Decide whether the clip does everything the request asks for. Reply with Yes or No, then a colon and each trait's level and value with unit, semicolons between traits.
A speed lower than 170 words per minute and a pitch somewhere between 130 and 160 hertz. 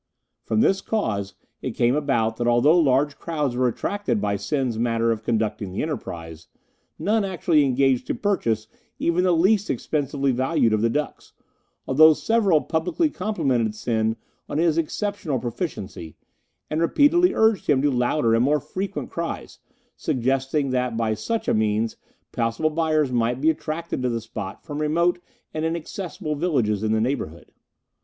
Yes: average, 155 wpm; medium, 140 Hz